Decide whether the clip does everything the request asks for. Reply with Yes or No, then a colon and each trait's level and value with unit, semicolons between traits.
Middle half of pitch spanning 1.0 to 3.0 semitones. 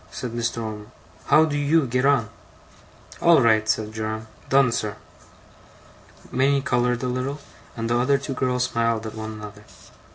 No: average, 3.5 semitones